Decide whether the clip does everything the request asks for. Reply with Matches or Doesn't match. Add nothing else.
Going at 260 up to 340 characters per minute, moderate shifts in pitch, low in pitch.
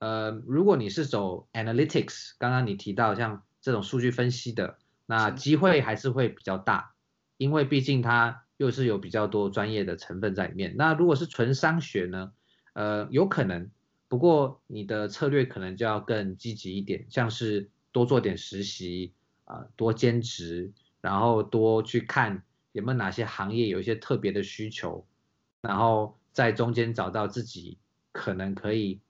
Matches